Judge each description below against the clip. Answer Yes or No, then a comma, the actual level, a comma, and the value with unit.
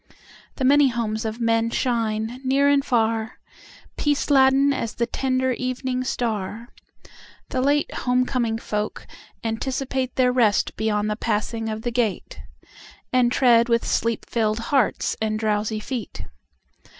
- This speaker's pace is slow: Yes, slow, 125 wpm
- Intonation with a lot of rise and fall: No, average, 2.8 semitones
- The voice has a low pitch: No, high, 235 Hz